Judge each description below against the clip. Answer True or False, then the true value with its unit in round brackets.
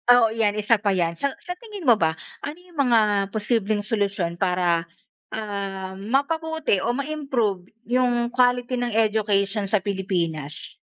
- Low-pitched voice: False (215 Hz)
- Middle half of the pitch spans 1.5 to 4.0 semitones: False (4.4 semitones)